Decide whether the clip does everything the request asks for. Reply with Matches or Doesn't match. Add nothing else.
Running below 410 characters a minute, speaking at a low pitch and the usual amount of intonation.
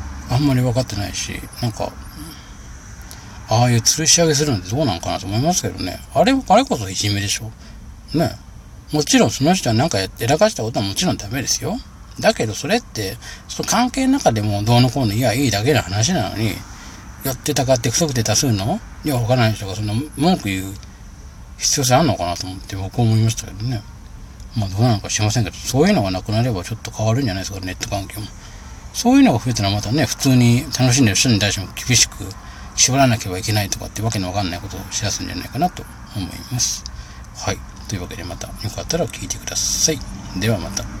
Doesn't match